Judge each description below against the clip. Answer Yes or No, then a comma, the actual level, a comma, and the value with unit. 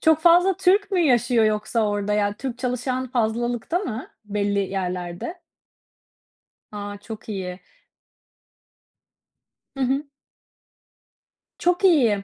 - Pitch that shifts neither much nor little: No, wide, 6.5 semitones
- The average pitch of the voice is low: No, high, 235 Hz